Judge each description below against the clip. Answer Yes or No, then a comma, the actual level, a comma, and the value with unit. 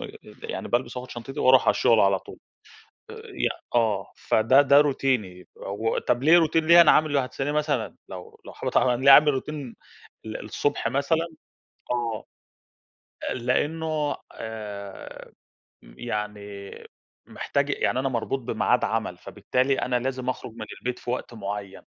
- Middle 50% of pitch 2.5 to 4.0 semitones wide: No, average, 4.6 semitones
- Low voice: Yes, low, 125 Hz